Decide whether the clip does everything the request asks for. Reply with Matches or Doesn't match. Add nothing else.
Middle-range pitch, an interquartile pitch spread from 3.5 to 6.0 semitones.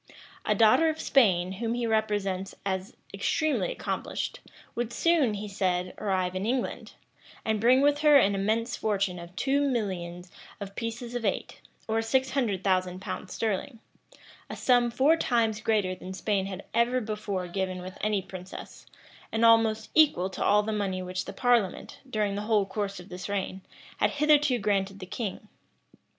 Doesn't match